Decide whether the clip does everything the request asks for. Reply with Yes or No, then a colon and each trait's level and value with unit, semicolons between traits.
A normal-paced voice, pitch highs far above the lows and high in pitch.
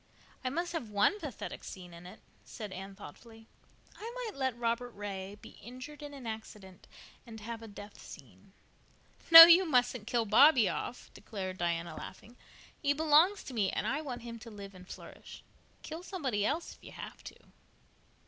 Yes: average, 175 wpm; wide, 6.2 semitones; high, 230 Hz